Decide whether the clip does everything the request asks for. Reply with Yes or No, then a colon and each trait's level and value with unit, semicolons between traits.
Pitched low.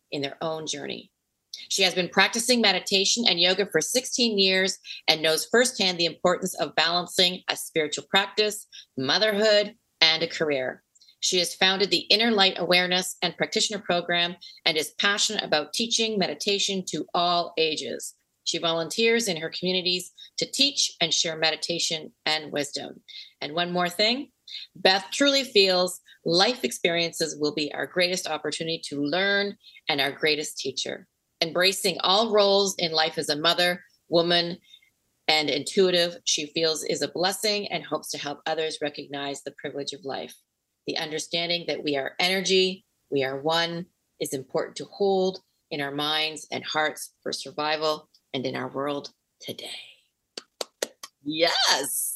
No: medium, 175 Hz